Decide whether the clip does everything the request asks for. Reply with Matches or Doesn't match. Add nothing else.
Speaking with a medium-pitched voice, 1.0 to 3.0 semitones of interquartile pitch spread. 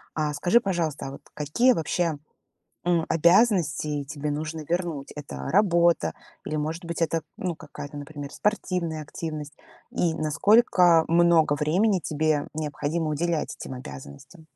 Matches